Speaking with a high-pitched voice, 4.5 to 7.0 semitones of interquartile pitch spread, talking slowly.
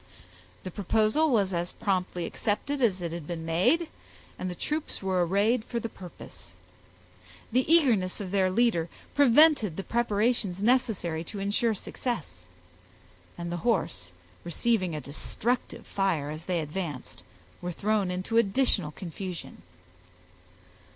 Yes: high, 195 Hz; average, 5.3 semitones; slow, 130 wpm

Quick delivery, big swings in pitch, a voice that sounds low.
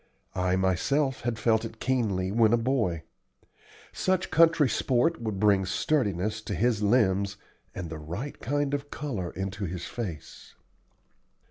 No: average, 140 wpm; wide, 5.7 semitones; low, 110 Hz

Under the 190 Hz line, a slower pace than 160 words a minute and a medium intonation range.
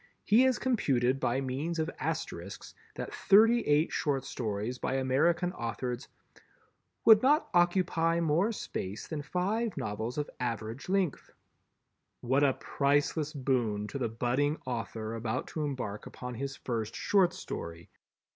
No: medium, 140 Hz; slow, 135 wpm; wide, 6.2 semitones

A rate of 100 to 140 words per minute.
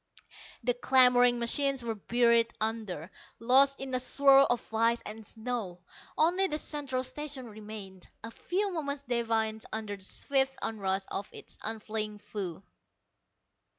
Yes: slow, 135 wpm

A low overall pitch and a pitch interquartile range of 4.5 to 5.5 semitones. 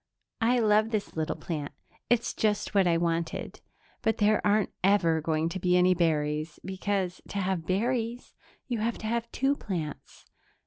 No: high, 190 Hz; average, 4.8 semitones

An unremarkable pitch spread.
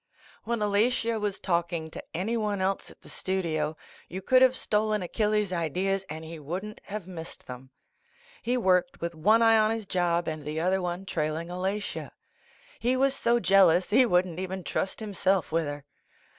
Yes: average, 4.0 semitones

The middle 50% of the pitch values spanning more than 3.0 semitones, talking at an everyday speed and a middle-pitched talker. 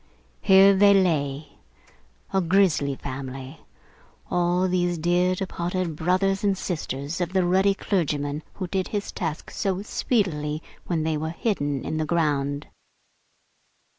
No: average, 4.2 semitones; slow, 130 wpm; medium, 175 Hz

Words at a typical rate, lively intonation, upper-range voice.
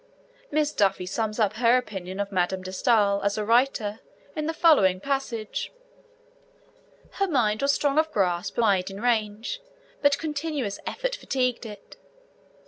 Yes: average, 150 wpm; wide, 5.9 semitones; high, 225 Hz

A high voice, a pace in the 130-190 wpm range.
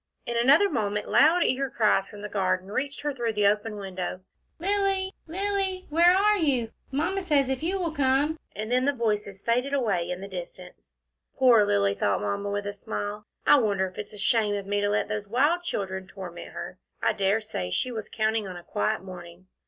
No: high, 215 Hz; fast, 205 wpm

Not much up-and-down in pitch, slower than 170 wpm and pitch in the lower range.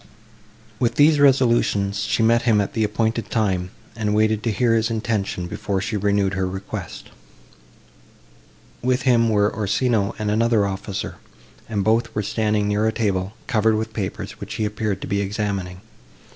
Yes: narrow, 2.2 semitones; average, 160 wpm; low, 110 Hz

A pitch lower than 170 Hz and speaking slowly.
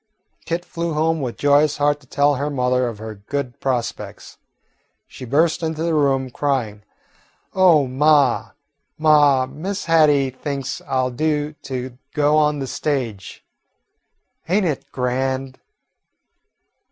Yes: medium, 140 Hz; slow, 130 wpm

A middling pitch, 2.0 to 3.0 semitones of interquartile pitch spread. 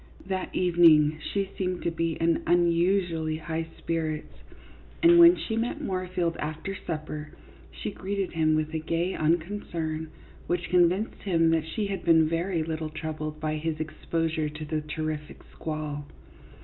Yes: medium, 165 Hz; narrow, 2.4 semitones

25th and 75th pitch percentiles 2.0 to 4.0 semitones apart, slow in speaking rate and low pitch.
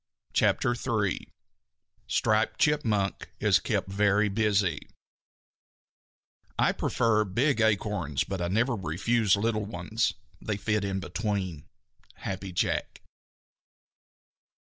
Yes: narrow, 2.5 semitones; slow, 100 wpm; low, 105 Hz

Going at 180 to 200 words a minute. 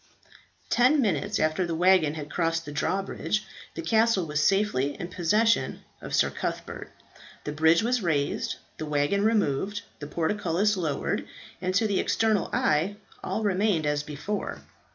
No: average, 150 wpm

